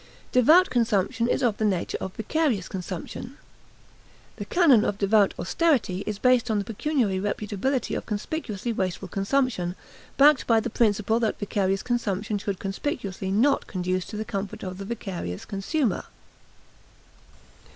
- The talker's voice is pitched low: No, high, 210 Hz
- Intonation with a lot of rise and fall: No, average, 4.1 semitones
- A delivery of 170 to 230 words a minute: No, average, 140 wpm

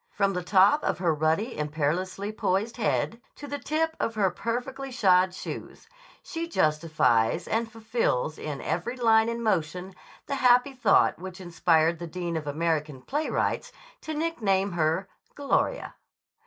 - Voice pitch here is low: No, high, 190 Hz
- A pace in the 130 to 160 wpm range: Yes, average, 145 wpm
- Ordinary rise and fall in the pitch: No, wide, 6.5 semitones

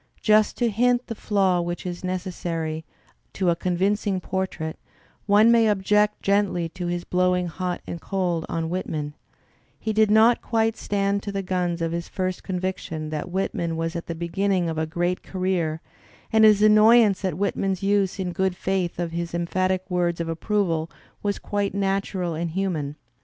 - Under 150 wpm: No, average, 175 wpm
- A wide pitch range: No, average, 2.9 semitones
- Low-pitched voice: No, medium, 185 Hz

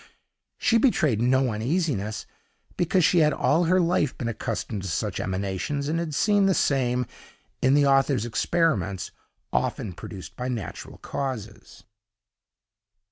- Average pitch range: No, wide, 7.1 semitones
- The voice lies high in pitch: No, low, 135 Hz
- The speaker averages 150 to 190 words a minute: No, slow, 135 wpm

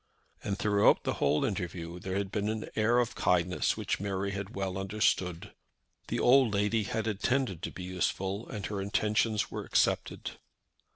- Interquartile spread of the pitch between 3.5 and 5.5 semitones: No, narrow, 2.4 semitones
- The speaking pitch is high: No, low, 100 Hz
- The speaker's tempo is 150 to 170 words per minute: Yes, average, 165 wpm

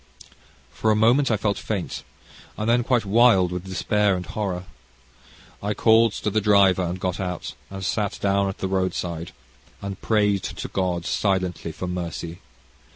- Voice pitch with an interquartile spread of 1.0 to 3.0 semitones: Yes, average, 2.7 semitones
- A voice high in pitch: No, low, 100 Hz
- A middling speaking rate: Yes, average, 165 wpm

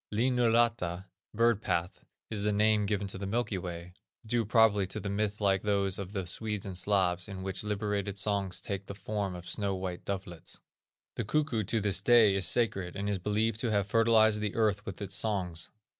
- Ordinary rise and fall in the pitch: No, narrow, 2.2 semitones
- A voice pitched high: No, low, 100 Hz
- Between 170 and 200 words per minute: Yes, average, 195 wpm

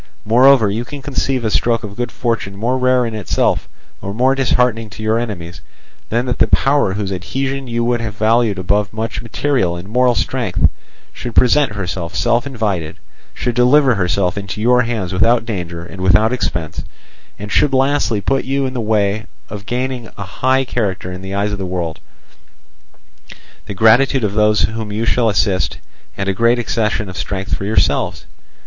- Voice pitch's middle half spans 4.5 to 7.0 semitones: No, average, 3.9 semitones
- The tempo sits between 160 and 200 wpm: Yes, average, 180 wpm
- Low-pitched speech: Yes, low, 110 Hz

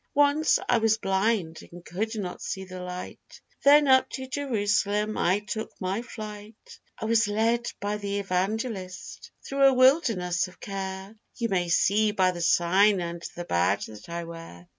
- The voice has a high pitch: Yes, high, 205 Hz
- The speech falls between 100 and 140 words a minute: No, average, 165 wpm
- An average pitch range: Yes, average, 3.7 semitones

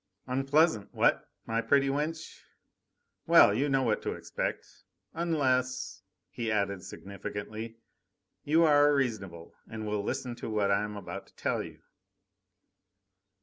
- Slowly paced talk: Yes, slow, 130 wpm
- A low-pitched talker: Yes, low, 115 Hz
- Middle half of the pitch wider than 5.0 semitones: Yes, wide, 5.5 semitones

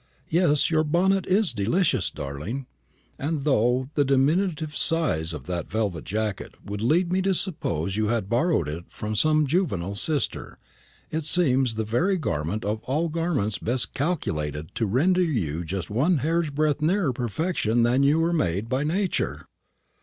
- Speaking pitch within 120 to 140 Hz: Yes, low, 135 Hz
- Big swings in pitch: Yes, wide, 8.0 semitones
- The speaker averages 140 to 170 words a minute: Yes, average, 160 wpm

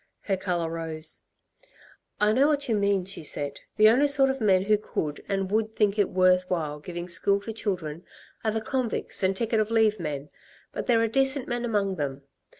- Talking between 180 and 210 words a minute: Yes, average, 200 wpm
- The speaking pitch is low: No, high, 200 Hz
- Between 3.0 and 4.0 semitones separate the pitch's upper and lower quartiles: No, average, 4.4 semitones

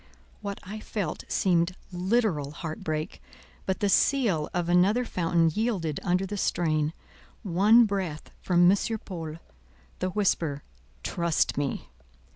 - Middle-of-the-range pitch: Yes, medium, 180 Hz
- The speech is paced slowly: Yes, slow, 125 wpm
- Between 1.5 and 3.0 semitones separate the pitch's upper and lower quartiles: No, average, 3.7 semitones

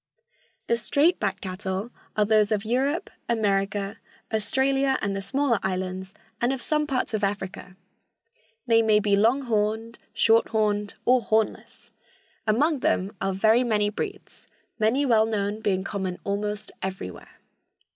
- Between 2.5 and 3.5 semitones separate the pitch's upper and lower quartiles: Yes, average, 3.2 semitones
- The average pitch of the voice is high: Yes, high, 215 Hz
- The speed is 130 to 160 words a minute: Yes, average, 140 wpm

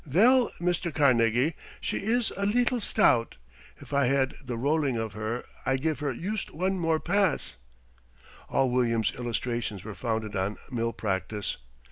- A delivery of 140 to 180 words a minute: Yes, average, 150 wpm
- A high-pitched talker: No, low, 130 Hz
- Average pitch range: No, wide, 7.1 semitones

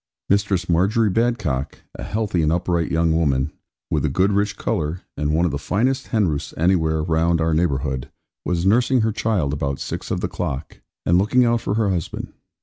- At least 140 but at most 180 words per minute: No, average, 195 wpm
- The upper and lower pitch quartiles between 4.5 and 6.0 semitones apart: Yes, average, 5.0 semitones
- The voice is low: Yes, very low, 85 Hz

